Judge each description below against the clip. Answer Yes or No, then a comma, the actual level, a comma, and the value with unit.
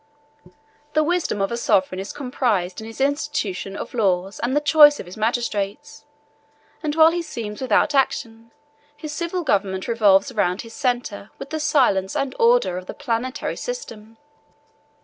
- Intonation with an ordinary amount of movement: No, wide, 6.5 semitones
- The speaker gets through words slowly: No, average, 155 wpm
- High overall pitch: Yes, high, 235 Hz